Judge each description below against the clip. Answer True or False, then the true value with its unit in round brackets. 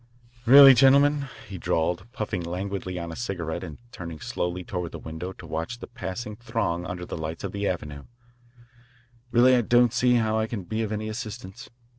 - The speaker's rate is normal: True (185 wpm)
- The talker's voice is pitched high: False (100 Hz)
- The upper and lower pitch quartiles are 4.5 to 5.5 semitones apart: True (5.2 semitones)